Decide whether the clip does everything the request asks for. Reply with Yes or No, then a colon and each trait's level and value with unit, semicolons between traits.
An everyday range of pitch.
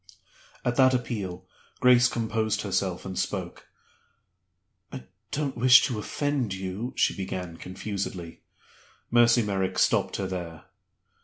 Yes: average, 4.7 semitones